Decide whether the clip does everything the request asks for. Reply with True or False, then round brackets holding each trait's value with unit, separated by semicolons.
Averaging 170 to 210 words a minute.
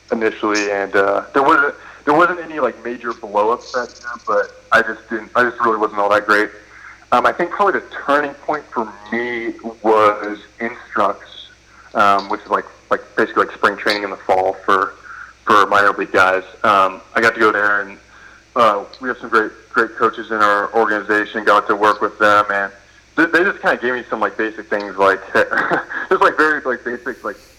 True (200 wpm)